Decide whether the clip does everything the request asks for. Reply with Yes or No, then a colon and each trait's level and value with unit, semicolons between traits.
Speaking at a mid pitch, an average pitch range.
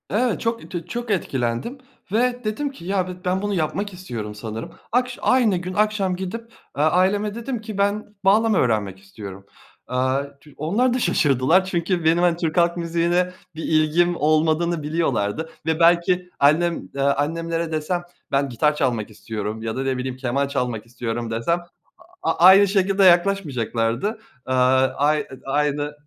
No: medium, 165 Hz; wide, 6.5 semitones